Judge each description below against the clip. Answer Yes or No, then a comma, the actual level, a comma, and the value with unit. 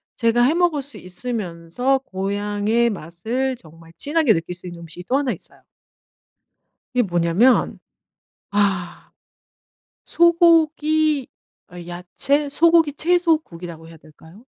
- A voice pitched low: No, high, 230 Hz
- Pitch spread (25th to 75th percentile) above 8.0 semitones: Yes, wide, 8.8 semitones